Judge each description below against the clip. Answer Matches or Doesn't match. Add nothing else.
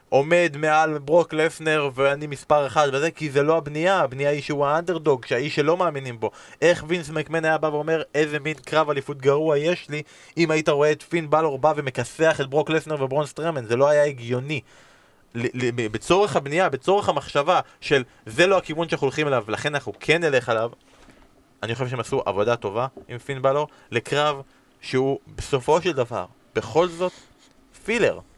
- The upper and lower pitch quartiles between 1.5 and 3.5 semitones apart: Matches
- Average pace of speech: Doesn't match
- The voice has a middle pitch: Matches